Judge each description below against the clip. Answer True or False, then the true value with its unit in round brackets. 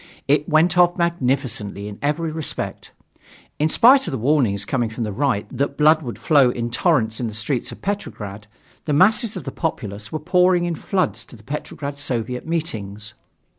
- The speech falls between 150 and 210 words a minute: True (180 wpm)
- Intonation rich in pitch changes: True (6.7 semitones)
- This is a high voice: False (140 Hz)